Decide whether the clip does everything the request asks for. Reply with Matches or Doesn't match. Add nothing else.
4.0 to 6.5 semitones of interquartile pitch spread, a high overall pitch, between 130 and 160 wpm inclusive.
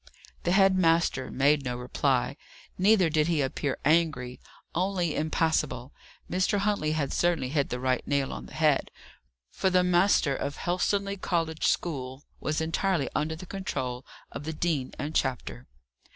Doesn't match